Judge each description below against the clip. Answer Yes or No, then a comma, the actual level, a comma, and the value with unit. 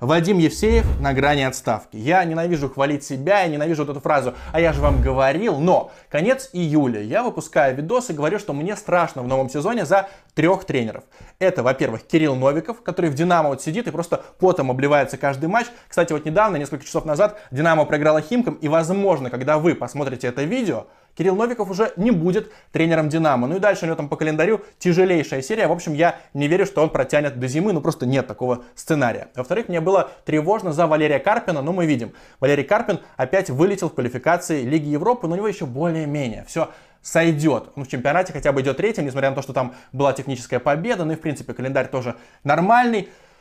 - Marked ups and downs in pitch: No, average, 4.7 semitones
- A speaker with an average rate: No, fast, 205 wpm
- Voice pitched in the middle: Yes, medium, 160 Hz